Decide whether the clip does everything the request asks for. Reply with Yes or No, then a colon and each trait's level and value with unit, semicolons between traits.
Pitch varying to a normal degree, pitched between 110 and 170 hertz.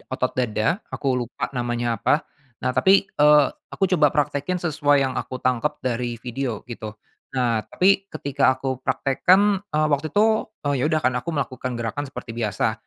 Yes: average, 3.9 semitones; low, 135 Hz